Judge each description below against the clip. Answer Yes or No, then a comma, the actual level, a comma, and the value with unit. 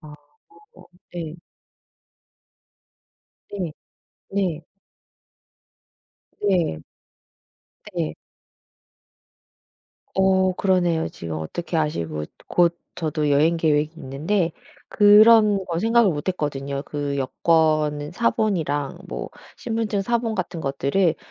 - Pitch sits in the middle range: Yes, medium, 165 Hz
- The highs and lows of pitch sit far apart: No, average, 4.7 semitones